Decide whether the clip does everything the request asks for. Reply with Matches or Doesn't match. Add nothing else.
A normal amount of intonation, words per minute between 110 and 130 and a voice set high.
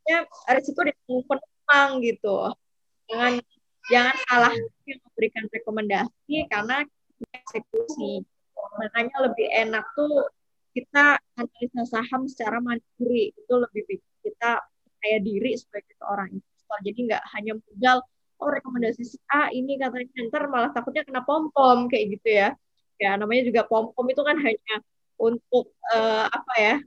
Doesn't match